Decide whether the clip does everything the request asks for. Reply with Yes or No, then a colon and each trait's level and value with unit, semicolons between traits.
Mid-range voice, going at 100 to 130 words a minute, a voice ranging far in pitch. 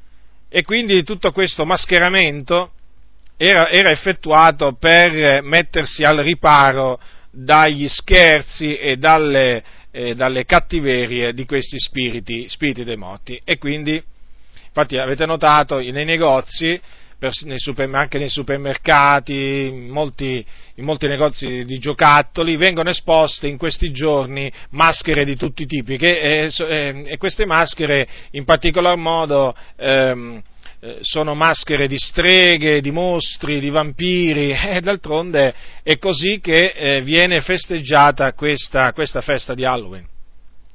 No: medium, 150 Hz; average, 120 wpm; average, 3.5 semitones